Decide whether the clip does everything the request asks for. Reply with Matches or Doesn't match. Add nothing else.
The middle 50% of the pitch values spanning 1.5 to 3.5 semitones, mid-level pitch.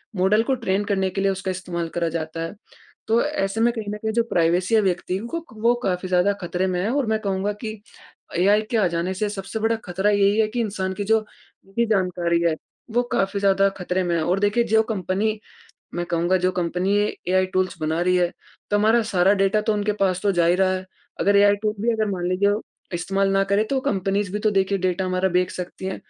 Doesn't match